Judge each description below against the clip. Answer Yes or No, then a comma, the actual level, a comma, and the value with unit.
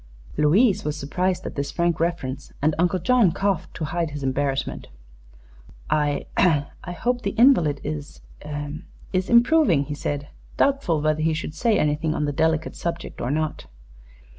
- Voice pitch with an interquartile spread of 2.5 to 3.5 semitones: No, average, 4.0 semitones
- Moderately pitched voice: Yes, medium, 160 Hz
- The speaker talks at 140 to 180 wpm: Yes, average, 155 wpm